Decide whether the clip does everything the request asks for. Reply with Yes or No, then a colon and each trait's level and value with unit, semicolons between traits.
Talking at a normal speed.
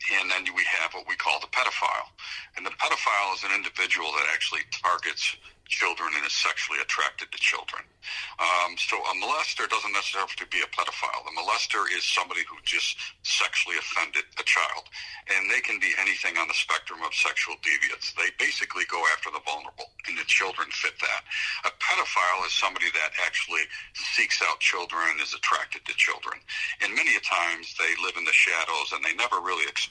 Yes: average, 195 wpm